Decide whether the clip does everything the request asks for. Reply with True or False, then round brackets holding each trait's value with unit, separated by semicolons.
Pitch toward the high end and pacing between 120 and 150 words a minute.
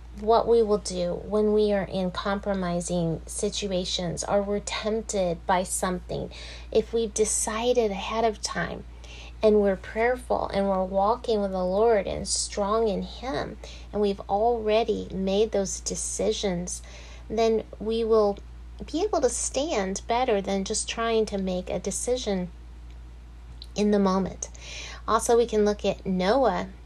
True (200 Hz; 145 wpm)